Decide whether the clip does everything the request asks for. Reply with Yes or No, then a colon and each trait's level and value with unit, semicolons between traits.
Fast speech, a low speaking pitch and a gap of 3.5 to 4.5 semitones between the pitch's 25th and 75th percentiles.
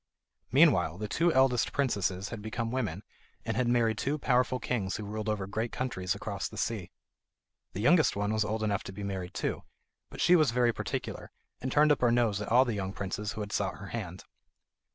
Yes: fast, 210 wpm; low, 110 Hz; average, 3.8 semitones